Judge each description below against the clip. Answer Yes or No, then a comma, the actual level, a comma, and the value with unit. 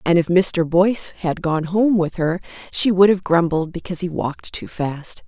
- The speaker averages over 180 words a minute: Yes, fast, 205 wpm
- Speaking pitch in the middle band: Yes, medium, 175 Hz